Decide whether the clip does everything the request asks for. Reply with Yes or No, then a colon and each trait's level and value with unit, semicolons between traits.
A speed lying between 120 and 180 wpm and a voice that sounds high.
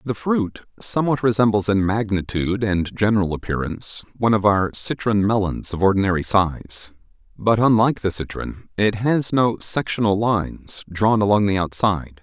No: average, 145 wpm; low, 100 Hz